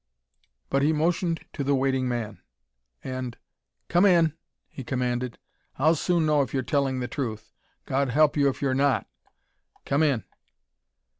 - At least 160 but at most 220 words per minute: No, average, 150 wpm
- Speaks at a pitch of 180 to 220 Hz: No, low, 135 Hz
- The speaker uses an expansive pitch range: No, average, 3.2 semitones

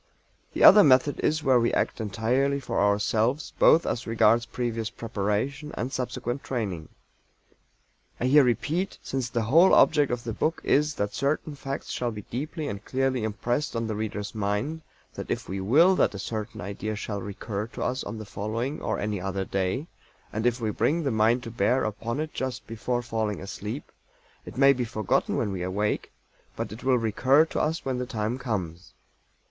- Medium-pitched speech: No, low, 115 Hz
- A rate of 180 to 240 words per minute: Yes, average, 185 wpm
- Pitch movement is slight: No, average, 4.1 semitones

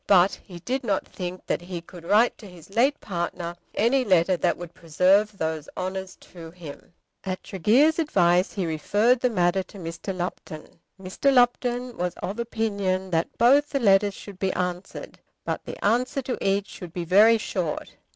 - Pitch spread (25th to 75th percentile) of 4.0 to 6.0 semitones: Yes, average, 4.4 semitones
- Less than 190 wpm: Yes, average, 180 wpm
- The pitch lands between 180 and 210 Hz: Yes, high, 190 Hz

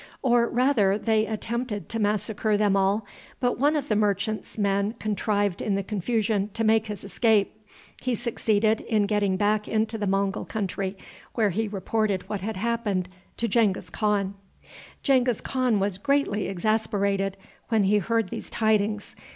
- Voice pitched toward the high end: Yes, high, 210 Hz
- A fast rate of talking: No, average, 155 wpm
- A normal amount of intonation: No, narrow, 2.1 semitones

